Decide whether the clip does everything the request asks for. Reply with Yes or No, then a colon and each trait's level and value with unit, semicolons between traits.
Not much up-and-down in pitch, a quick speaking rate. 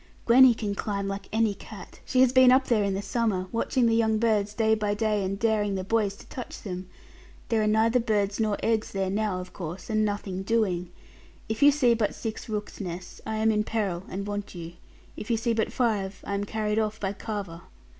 Yes: narrow, 2.3 semitones; fast, 220 wpm